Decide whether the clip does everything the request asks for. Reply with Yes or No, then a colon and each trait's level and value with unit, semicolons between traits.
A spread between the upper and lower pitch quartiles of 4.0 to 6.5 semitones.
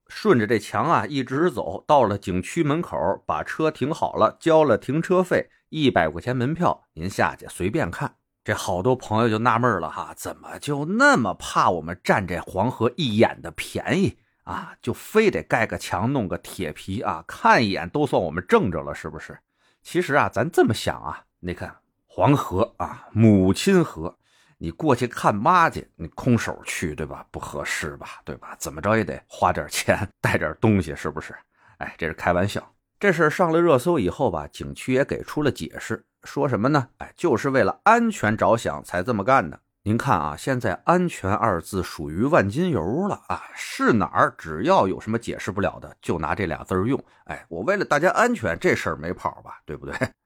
No: wide, 9.0 semitones